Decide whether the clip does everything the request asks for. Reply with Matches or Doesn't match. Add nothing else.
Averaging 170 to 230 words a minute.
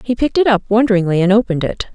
Doesn't match